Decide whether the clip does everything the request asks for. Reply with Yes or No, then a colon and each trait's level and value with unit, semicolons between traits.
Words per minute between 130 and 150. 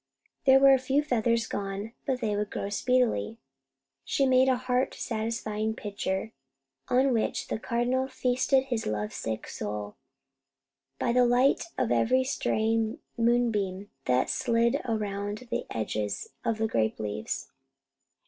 Yes: average, 140 wpm